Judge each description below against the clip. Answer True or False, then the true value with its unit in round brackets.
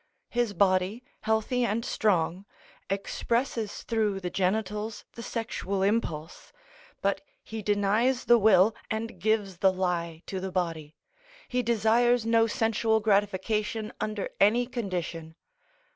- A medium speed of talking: False (120 wpm)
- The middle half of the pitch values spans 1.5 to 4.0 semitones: True (3.2 semitones)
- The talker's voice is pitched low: False (210 Hz)